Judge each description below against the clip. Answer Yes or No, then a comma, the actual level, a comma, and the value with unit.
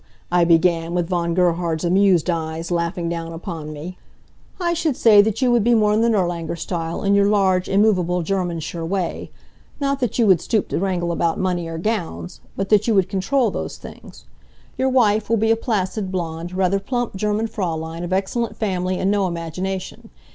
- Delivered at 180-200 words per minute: Yes, average, 190 wpm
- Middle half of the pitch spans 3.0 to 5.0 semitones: Yes, average, 3.7 semitones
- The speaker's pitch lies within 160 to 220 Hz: Yes, medium, 185 Hz